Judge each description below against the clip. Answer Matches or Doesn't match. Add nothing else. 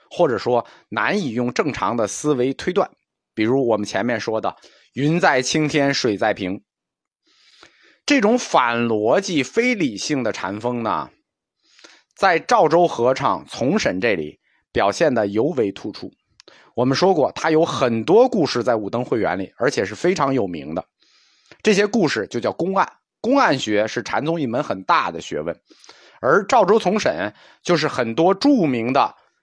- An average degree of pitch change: Doesn't match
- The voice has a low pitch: Doesn't match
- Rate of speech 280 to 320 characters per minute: Doesn't match